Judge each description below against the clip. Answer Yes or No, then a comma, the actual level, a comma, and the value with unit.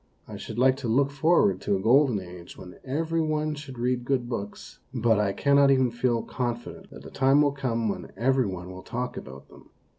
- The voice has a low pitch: Yes, low, 125 Hz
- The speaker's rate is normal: No, fast, 220 wpm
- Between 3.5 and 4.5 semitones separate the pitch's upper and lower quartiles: Yes, average, 4.1 semitones